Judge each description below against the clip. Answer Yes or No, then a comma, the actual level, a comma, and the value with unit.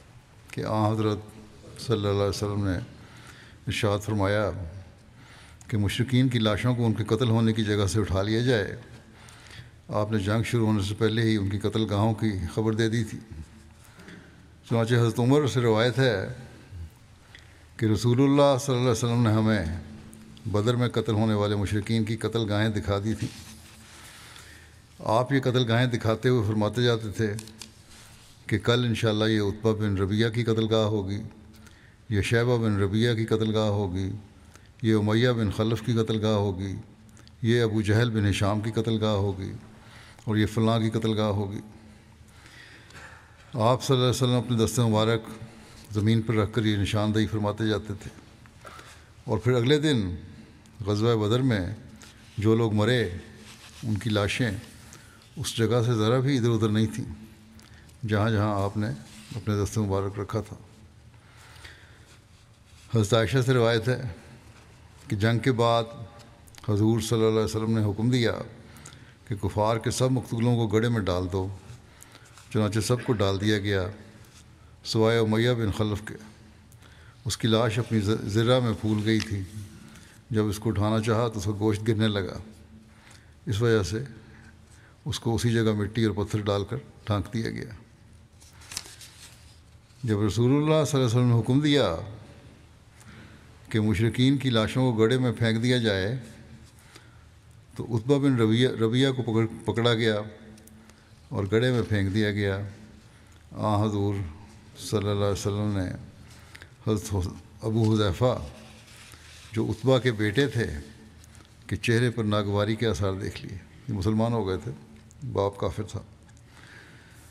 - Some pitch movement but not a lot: No, narrow, 1.8 semitones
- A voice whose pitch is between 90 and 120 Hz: Yes, low, 110 Hz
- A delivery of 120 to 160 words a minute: Yes, average, 155 wpm